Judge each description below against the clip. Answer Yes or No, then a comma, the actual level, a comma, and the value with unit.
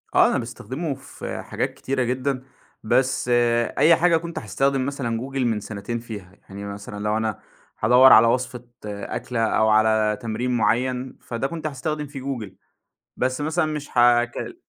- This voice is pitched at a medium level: No, low, 125 Hz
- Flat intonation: No, average, 3.8 semitones